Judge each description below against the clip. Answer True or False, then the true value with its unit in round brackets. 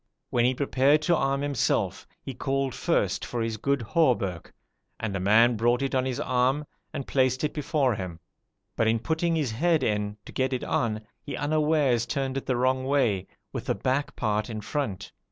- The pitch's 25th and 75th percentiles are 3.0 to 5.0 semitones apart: True (3.9 semitones)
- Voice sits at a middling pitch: False (130 Hz)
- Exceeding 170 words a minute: True (190 wpm)